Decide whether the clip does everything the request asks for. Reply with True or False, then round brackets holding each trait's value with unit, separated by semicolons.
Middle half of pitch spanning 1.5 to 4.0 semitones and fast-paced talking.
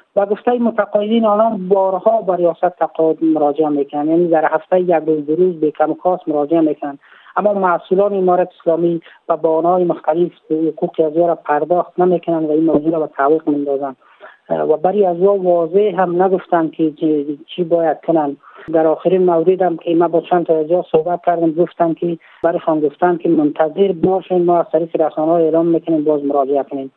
True (2.4 semitones; 175 wpm)